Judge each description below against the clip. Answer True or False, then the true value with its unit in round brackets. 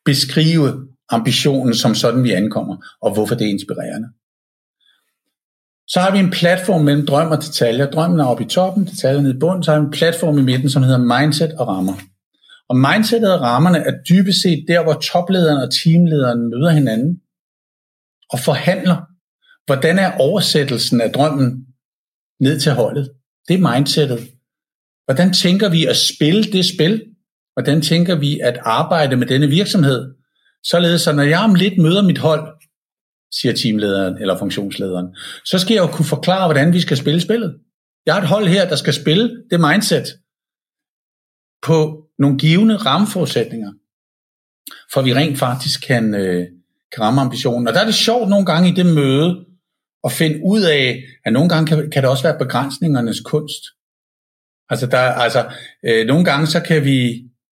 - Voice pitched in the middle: True (150 Hz)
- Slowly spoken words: False (170 wpm)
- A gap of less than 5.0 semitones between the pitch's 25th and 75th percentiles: False (5.5 semitones)